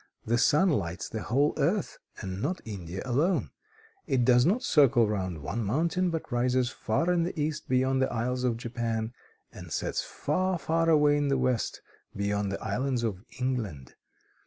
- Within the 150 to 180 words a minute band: Yes, average, 170 wpm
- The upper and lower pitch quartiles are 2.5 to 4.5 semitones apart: No, average, 5.2 semitones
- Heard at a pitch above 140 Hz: No, low, 125 Hz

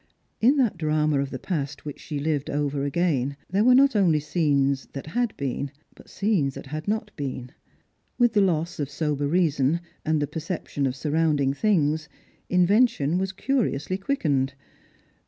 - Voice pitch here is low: No, medium, 155 Hz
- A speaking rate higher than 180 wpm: No, average, 160 wpm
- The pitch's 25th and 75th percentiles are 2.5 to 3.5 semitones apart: No, average, 5.1 semitones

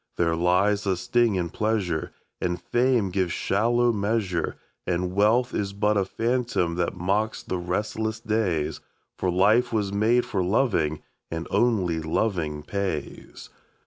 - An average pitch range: Yes, average, 3.9 semitones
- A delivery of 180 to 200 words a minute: No, average, 140 wpm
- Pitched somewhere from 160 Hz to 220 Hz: No, low, 100 Hz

